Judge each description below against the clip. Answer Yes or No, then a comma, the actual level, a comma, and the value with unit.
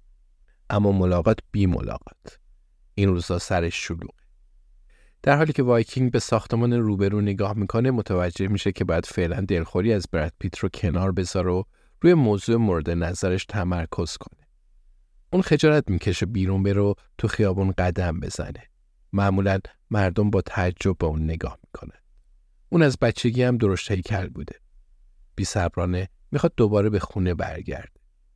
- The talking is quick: No, average, 140 wpm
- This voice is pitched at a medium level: No, low, 100 Hz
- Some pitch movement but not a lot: Yes, average, 3.7 semitones